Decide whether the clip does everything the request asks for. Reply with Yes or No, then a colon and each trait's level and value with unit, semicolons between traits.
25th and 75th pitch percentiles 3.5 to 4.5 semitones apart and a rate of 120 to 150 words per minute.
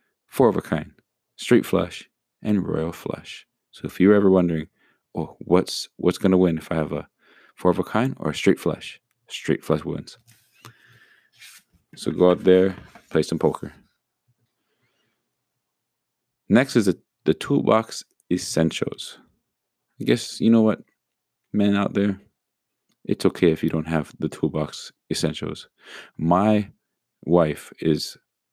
Yes: average, 3.9 semitones; average, 145 wpm